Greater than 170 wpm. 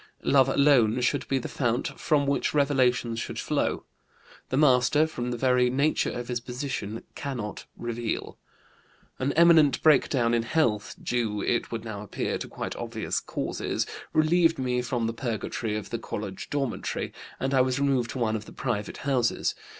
No: average, 165 wpm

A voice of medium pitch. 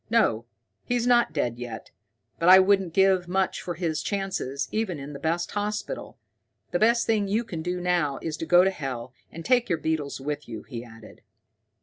Yes: medium, 175 Hz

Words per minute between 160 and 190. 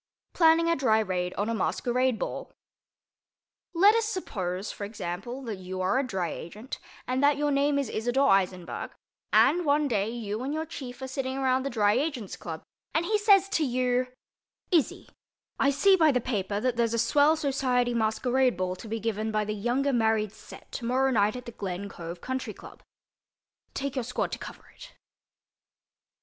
Yes: average, 180 wpm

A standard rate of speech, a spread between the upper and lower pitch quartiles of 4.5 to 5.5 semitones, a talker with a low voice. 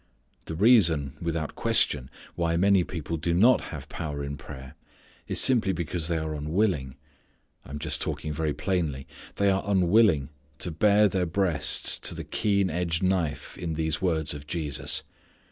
No: average, 160 wpm; average, 4.0 semitones; very low, 85 Hz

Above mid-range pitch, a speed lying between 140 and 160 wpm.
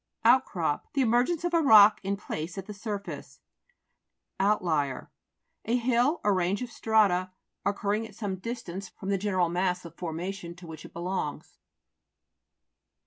Yes: high, 195 Hz; average, 145 wpm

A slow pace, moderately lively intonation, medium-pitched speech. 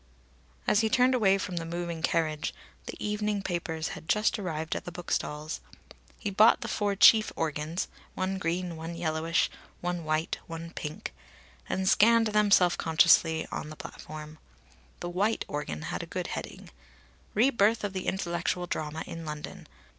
No: average, 160 wpm; average, 3.9 semitones; medium, 175 Hz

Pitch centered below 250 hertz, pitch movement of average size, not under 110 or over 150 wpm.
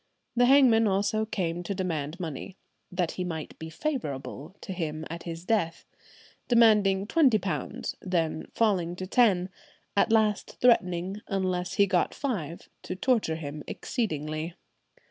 Yes: medium, 185 Hz; average, 4.7 semitones; average, 140 wpm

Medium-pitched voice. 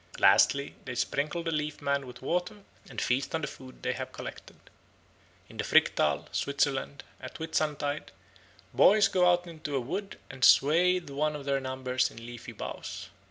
Yes: medium, 145 Hz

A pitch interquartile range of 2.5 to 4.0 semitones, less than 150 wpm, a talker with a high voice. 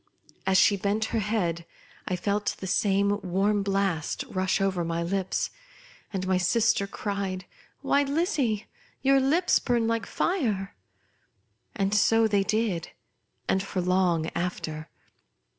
Yes: average, 3.0 semitones; slow, 135 wpm; high, 200 Hz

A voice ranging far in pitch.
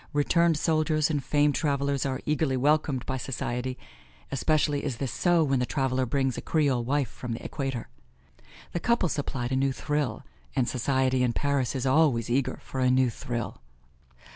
No: narrow, 2.6 semitones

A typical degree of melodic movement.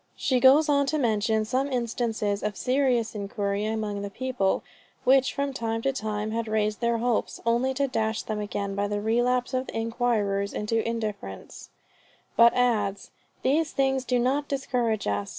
Yes: average, 3.5 semitones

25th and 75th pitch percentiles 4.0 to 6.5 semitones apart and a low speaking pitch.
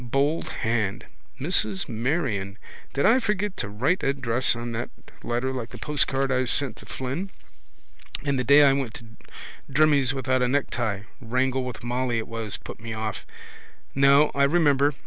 No: average, 3.2 semitones; low, 130 Hz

